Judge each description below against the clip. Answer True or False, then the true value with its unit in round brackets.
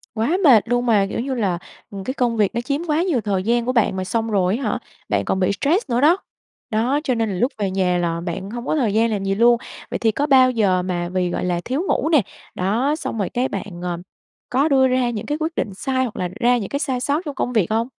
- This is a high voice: True (230 Hz)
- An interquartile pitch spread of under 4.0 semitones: False (5.1 semitones)